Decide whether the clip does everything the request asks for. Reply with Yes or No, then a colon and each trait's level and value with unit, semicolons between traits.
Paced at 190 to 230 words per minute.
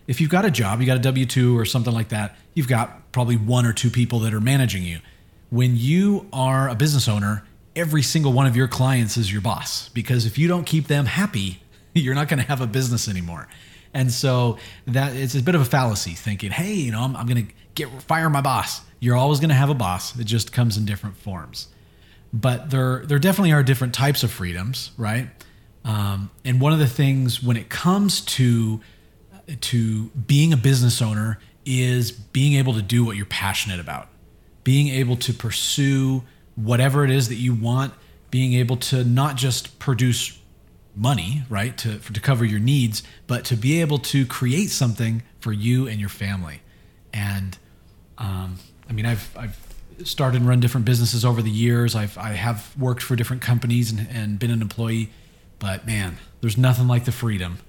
Yes: average, 200 wpm